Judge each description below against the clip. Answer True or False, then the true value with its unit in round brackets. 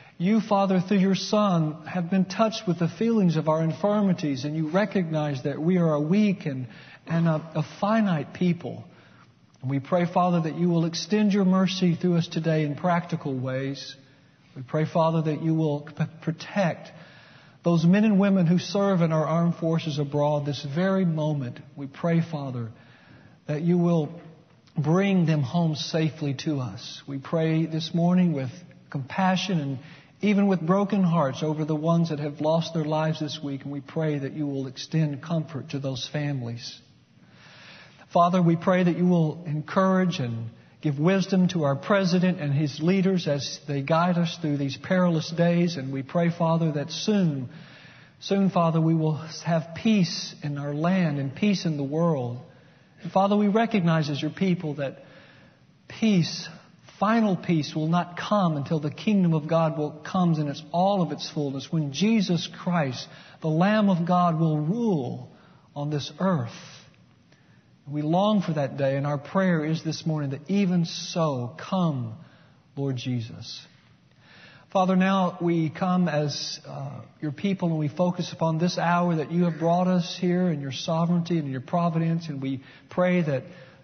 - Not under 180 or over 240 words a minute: False (170 wpm)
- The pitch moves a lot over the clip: False (3.4 semitones)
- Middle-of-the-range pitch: True (165 Hz)